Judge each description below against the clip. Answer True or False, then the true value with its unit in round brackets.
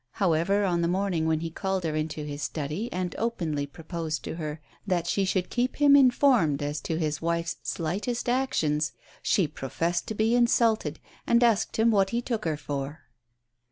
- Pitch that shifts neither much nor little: False (5.9 semitones)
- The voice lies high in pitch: False (170 Hz)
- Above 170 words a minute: True (180 wpm)